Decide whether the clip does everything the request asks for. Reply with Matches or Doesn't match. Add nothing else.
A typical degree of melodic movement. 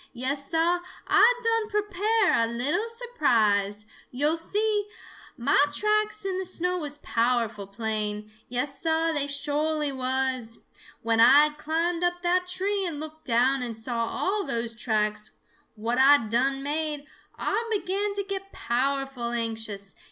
Doesn't match